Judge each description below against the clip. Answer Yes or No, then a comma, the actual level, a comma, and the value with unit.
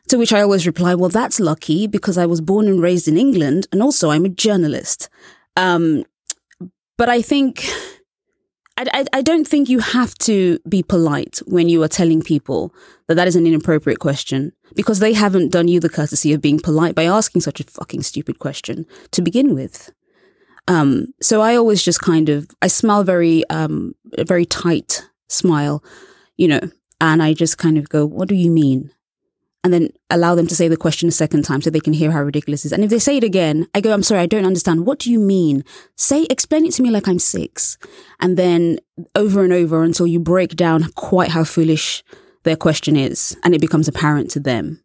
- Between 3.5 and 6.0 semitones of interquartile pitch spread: Yes, average, 4.4 semitones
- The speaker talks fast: Yes, fast, 210 wpm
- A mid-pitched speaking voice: Yes, medium, 175 Hz